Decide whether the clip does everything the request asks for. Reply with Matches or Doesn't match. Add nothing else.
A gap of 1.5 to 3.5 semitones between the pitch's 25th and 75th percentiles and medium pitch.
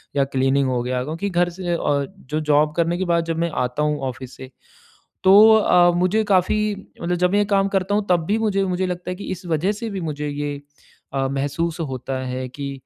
Doesn't match